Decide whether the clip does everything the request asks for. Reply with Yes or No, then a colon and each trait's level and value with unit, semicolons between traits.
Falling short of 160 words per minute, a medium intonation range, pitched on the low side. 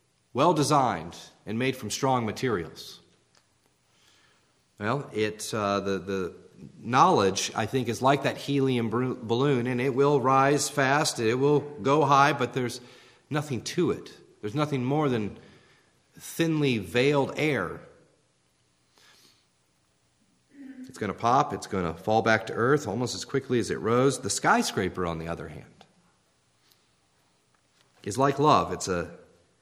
No: average, 140 wpm; wide, 6.2 semitones; low, 120 Hz